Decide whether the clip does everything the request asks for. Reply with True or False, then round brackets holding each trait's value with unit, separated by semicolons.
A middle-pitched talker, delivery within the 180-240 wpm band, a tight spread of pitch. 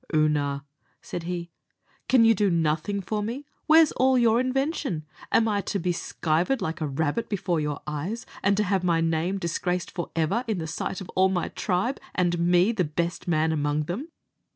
False (180 Hz; 185 wpm; 4.9 semitones)